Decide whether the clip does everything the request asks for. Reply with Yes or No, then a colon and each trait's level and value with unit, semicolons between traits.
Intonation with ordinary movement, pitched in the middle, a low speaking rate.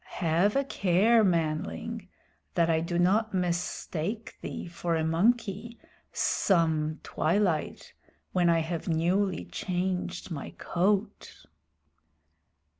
Yes: average, 3.5 semitones; medium, 180 Hz; slow, 105 wpm